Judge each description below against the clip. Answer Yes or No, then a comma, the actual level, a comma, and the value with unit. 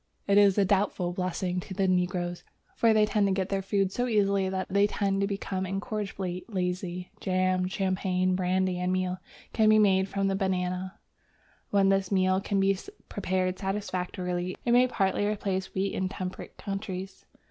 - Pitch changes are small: Yes, narrow, 1.3 semitones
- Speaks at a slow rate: No, average, 165 wpm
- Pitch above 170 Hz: Yes, high, 190 Hz